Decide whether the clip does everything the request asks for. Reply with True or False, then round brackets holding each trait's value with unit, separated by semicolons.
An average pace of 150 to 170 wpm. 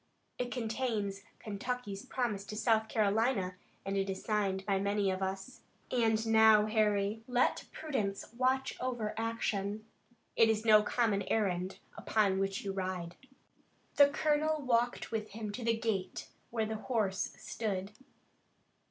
False (140 wpm)